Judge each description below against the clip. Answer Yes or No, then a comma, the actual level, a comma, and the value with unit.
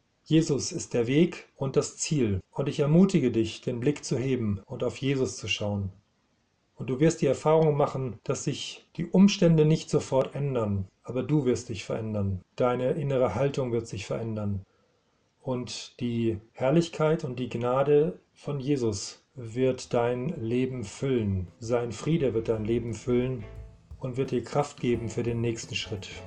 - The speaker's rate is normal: Yes, average, 160 wpm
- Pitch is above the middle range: No, low, 125 Hz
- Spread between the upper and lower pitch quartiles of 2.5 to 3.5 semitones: No, average, 4.3 semitones